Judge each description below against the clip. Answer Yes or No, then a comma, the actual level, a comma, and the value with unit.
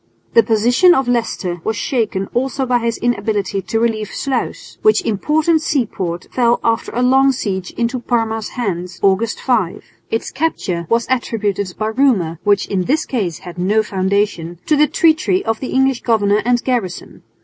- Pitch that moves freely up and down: No, average, 4.4 semitones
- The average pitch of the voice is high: Yes, high, 225 Hz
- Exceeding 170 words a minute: No, average, 165 wpm